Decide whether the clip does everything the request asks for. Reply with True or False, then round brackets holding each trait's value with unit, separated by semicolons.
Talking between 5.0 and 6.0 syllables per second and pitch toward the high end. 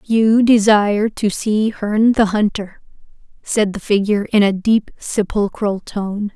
False (4.1 syllables/s; 210 Hz)